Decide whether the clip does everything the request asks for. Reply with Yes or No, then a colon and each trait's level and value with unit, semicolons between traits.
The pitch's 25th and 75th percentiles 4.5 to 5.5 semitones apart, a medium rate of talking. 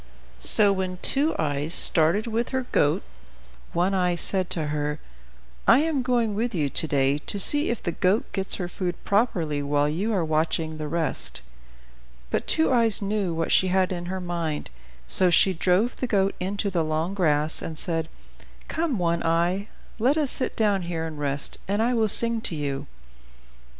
Yes: average, 5.1 semitones; average, 180 wpm